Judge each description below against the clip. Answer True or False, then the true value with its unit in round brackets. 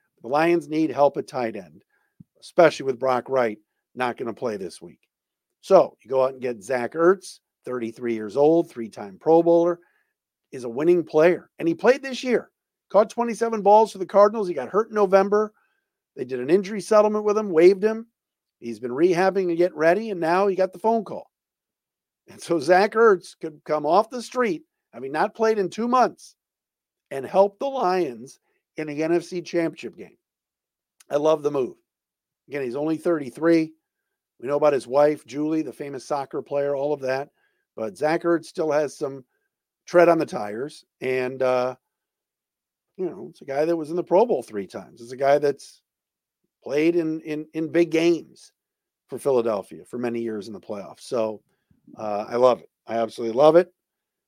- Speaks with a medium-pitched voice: True (165 Hz)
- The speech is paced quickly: False (190 wpm)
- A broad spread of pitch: True (5.8 semitones)